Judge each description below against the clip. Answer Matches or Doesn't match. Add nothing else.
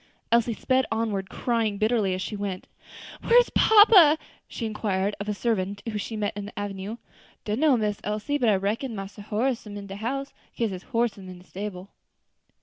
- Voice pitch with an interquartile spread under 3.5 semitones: Matches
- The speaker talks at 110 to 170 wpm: Doesn't match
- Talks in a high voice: Matches